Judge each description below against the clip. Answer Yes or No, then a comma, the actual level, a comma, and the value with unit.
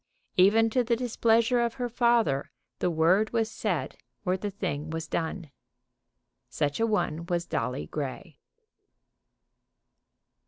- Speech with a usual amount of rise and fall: No, wide, 6.1 semitones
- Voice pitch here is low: No, high, 190 Hz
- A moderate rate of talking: No, slow, 125 wpm